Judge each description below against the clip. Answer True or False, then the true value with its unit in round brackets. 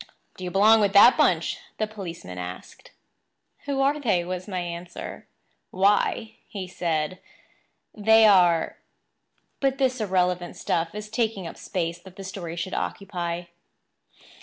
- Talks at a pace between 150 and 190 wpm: False (135 wpm)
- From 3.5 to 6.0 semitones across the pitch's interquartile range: True (3.8 semitones)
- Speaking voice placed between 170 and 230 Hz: True (185 Hz)